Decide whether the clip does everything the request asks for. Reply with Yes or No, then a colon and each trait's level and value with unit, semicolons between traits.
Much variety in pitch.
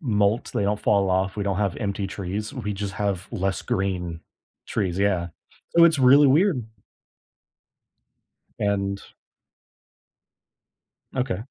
No: narrow, 2.5 semitones